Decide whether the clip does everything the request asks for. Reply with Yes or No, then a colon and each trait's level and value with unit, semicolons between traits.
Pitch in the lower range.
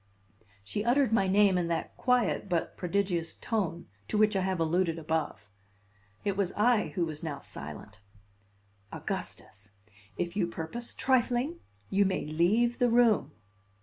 No: high, 190 Hz